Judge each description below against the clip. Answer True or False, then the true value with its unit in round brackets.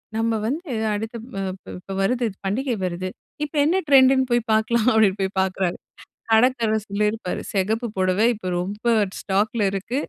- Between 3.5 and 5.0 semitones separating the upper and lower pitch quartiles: True (3.8 semitones)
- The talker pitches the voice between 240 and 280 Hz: False (220 Hz)